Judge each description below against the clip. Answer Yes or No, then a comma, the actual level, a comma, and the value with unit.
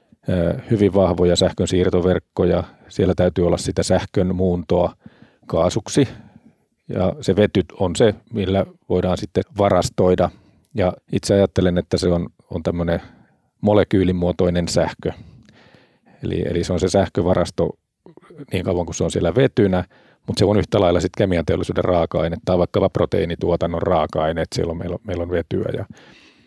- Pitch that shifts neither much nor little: No, narrow, 1.9 semitones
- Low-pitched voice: Yes, very low, 90 Hz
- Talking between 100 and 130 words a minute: No, average, 145 wpm